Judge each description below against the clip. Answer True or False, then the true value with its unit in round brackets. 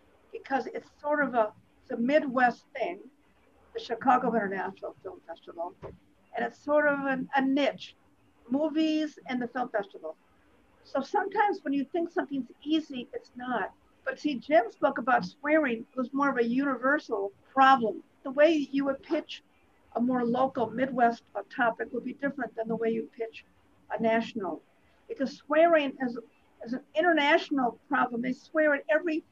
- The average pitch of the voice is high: True (265 Hz)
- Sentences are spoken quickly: False (160 wpm)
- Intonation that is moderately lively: True (4.0 semitones)